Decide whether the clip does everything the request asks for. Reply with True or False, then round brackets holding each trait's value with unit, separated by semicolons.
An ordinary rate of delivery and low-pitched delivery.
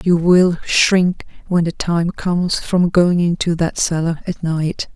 False (170 wpm; 175 Hz)